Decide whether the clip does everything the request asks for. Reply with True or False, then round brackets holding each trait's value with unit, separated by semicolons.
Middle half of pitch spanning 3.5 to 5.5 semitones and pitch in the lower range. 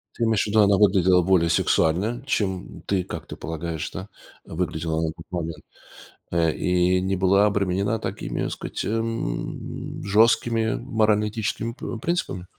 True (4.1 semitones; 95 Hz)